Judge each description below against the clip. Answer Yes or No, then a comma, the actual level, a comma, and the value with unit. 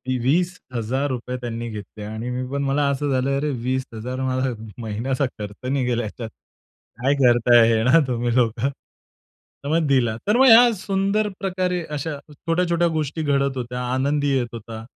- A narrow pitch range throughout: No, average, 3.7 semitones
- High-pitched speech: No, low, 130 Hz